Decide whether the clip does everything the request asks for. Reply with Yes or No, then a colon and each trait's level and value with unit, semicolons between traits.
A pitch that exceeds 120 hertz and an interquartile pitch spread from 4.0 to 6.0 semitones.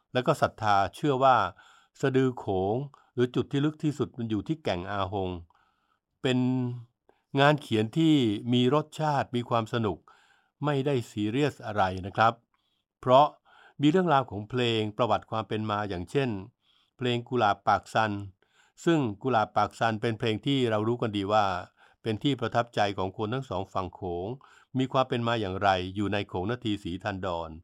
No: low, 115 Hz; average, 4.3 semitones